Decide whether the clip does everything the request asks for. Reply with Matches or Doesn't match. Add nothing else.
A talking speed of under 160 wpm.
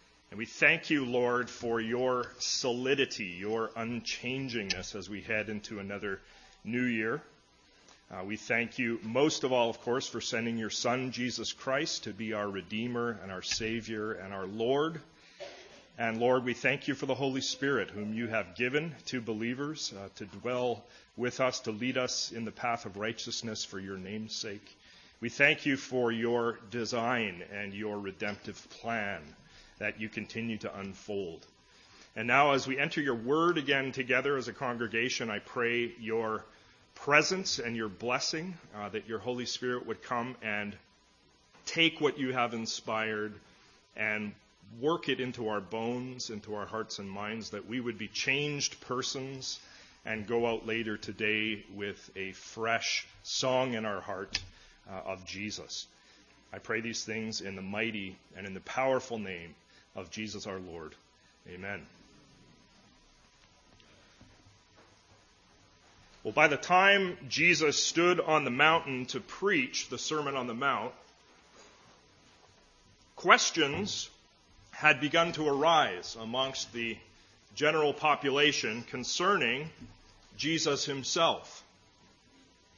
Matches